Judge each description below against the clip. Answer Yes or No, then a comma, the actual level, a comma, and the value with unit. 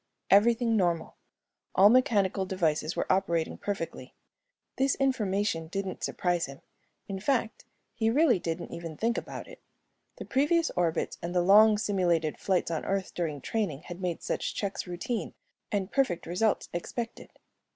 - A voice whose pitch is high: Yes, high, 195 Hz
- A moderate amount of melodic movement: Yes, average, 4.4 semitones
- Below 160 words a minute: Yes, average, 145 wpm